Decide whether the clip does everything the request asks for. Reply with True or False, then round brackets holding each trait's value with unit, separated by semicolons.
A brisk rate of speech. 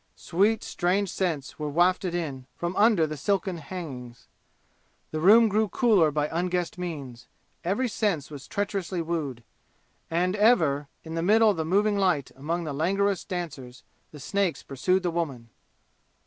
False (150 wpm)